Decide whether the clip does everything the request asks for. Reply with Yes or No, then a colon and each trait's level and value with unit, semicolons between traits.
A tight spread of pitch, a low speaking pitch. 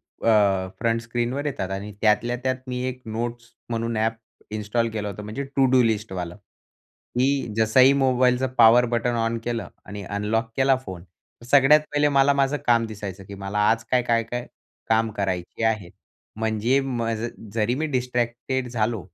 No: average, 3.0 semitones; low, 115 Hz